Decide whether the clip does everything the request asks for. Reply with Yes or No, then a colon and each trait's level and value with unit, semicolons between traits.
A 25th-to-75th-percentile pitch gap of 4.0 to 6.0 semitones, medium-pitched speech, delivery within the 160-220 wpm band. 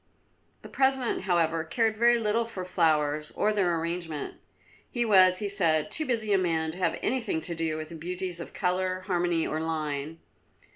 Yes: average, 4.4 semitones; medium, 180 Hz; average, 180 wpm